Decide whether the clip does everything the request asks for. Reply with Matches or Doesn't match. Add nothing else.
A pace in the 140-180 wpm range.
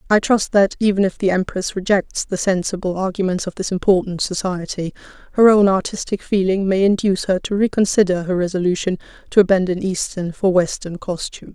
Matches